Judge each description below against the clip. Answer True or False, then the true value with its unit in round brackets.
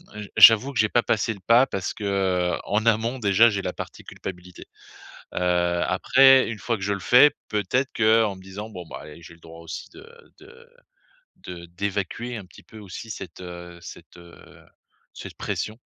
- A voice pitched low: True (105 Hz)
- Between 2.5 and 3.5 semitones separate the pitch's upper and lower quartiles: False (4.1 semitones)